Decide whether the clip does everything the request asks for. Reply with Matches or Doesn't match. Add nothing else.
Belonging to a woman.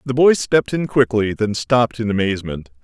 Doesn't match